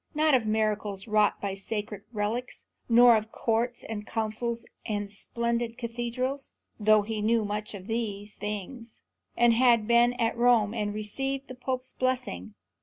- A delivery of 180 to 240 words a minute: No, average, 150 wpm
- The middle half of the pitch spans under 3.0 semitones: Yes, narrow, 2.4 semitones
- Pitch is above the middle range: Yes, high, 225 Hz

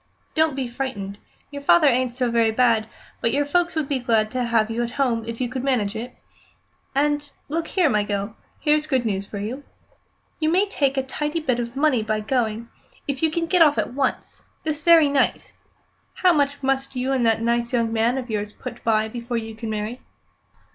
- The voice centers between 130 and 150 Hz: No, very high, 250 Hz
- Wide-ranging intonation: No, average, 4.2 semitones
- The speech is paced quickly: Yes, fast, 210 wpm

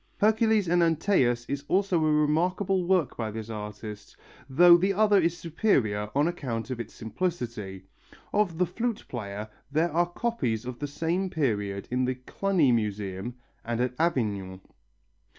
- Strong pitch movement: Yes, wide, 8.0 semitones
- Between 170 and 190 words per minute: No, average, 150 wpm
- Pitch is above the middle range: No, medium, 145 Hz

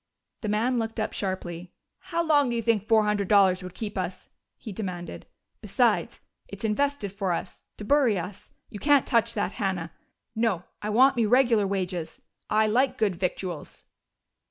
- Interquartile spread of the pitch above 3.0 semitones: Yes, average, 3.8 semitones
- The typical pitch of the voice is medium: No, high, 210 Hz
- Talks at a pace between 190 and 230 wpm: No, average, 170 wpm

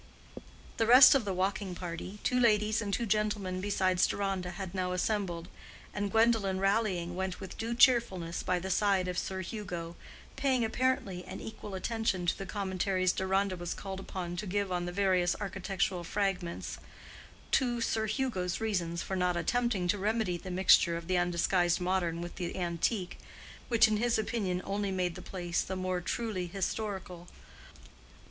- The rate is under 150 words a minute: No, average, 160 wpm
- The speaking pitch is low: No, high, 190 Hz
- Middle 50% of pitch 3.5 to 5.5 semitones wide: No, average, 2.9 semitones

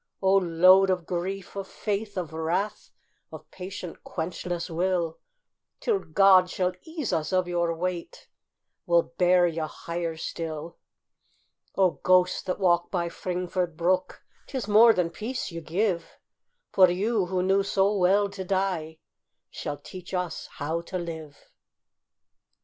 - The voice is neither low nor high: Yes, medium, 180 Hz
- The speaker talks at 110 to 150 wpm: Yes, average, 140 wpm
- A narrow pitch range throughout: Yes, narrow, 2.3 semitones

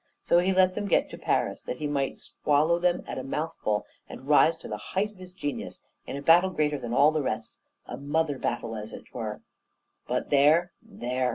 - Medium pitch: Yes, medium, 150 Hz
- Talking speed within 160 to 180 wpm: No, fast, 205 wpm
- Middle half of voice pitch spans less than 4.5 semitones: No, average, 5.1 semitones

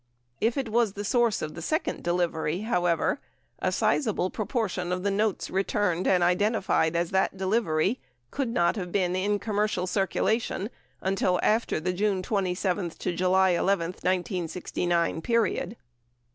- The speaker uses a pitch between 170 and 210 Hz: Yes, high, 190 Hz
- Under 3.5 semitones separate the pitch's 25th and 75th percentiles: Yes, average, 3.1 semitones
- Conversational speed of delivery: Yes, average, 145 wpm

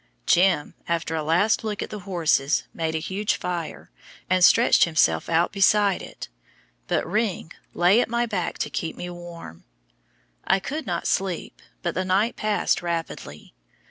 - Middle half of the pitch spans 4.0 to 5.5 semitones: No, average, 3.6 semitones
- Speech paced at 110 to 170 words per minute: Yes, average, 160 wpm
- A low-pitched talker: No, medium, 180 Hz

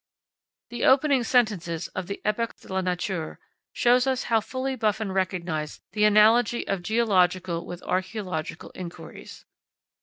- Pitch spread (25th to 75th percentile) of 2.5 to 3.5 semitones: No, average, 4.4 semitones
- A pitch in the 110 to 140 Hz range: No, high, 205 Hz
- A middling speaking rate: No, slow, 130 wpm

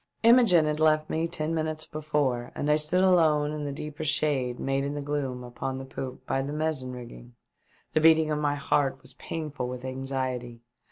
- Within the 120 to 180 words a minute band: No, average, 200 wpm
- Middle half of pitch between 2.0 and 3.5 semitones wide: Yes, average, 2.9 semitones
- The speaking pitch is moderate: Yes, medium, 145 Hz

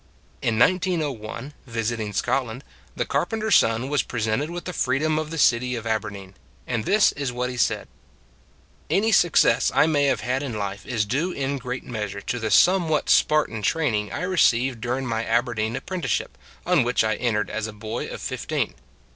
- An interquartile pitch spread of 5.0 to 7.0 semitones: Yes, average, 5.3 semitones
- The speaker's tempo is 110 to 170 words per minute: No, average, 180 wpm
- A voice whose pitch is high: No, low, 125 Hz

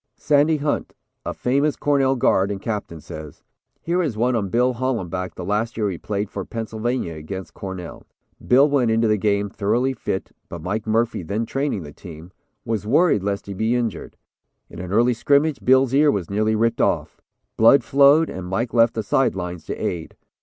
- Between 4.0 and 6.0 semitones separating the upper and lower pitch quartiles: Yes, average, 5.1 semitones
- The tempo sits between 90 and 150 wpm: No, average, 190 wpm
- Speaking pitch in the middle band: No, low, 110 Hz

